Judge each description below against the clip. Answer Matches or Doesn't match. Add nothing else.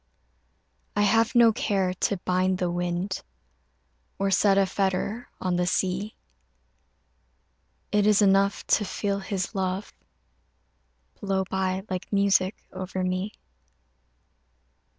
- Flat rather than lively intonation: Matches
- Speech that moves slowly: Matches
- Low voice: Doesn't match